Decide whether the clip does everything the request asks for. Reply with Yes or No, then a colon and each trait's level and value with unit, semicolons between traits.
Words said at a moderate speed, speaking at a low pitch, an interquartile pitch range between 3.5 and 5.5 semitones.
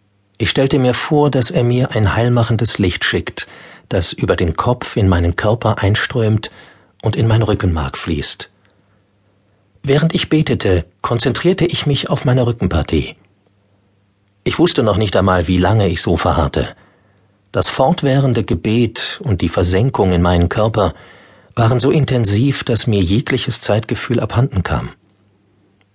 Yes: average, 140 wpm; low, 105 Hz; average, 3.9 semitones